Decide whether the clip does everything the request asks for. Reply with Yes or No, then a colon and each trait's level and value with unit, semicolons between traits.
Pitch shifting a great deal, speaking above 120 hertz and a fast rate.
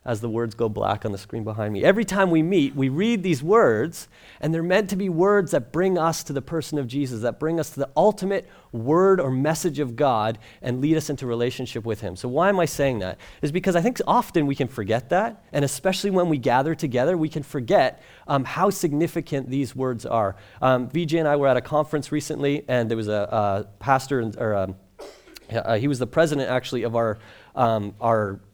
Yes: wide, 6.0 semitones; medium, 140 Hz; fast, 225 wpm